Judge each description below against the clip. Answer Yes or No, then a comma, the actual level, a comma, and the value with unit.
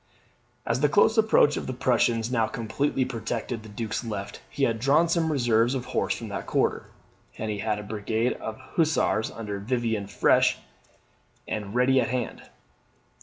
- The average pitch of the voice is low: Yes, low, 115 Hz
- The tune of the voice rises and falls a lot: No, average, 3.3 semitones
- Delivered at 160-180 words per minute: Yes, average, 170 wpm